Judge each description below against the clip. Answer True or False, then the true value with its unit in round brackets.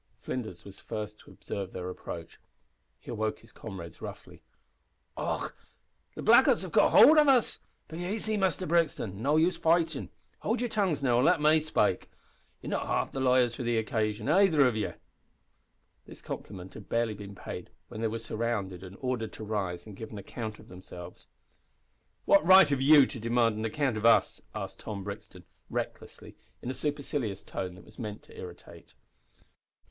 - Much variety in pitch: True (6.5 semitones)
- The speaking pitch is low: True (115 Hz)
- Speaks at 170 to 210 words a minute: True (180 wpm)